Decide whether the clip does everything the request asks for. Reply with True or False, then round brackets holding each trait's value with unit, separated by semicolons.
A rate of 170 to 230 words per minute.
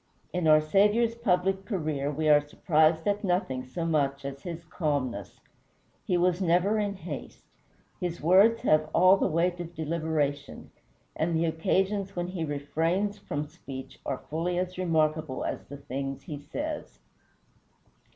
False (150 wpm)